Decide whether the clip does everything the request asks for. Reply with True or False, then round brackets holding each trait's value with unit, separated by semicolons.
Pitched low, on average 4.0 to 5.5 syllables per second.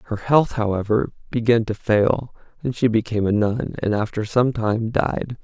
True (110 Hz; 4.7 syllables/s)